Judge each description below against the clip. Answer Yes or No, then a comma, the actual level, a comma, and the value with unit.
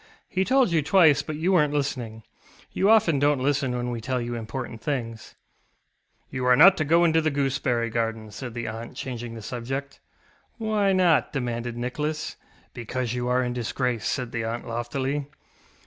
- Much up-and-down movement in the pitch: No, average, 4.1 semitones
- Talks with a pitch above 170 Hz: No, low, 130 Hz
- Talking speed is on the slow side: No, average, 175 wpm